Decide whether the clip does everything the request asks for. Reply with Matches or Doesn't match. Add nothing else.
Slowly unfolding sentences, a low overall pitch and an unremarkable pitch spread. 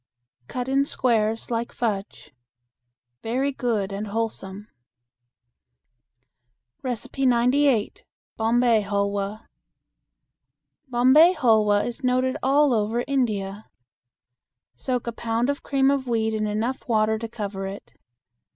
Doesn't match